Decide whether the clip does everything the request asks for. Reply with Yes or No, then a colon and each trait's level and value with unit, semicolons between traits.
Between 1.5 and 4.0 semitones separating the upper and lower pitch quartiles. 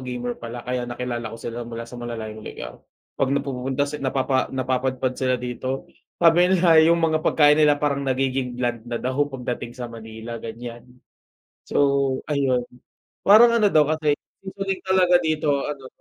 Yes: average, 3.5 semitones